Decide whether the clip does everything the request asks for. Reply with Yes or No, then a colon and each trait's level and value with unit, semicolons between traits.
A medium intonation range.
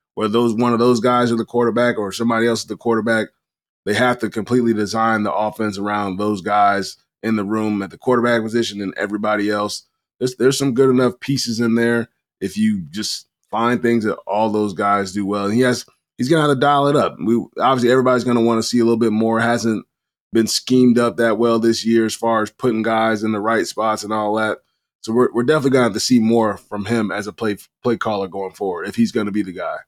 No: narrow, 2.2 semitones